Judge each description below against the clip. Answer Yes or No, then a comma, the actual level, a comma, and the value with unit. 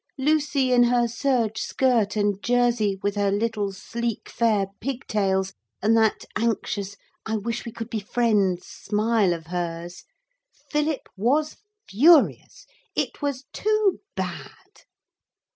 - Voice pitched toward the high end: Yes, high, 225 Hz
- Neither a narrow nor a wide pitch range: Yes, average, 3.5 semitones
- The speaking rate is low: Yes, slow, 125 wpm